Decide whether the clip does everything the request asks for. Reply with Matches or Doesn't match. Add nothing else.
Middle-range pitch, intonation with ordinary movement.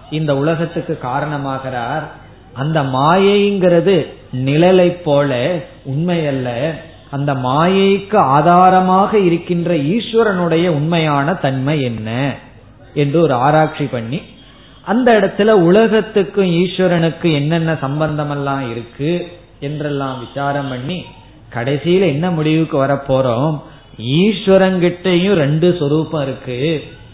Matches